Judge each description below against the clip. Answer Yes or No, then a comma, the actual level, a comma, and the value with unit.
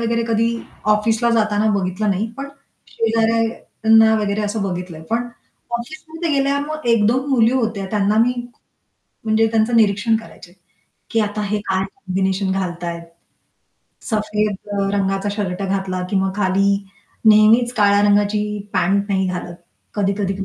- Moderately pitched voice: No, high, 210 Hz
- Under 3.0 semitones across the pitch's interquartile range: Yes, narrow, 2.6 semitones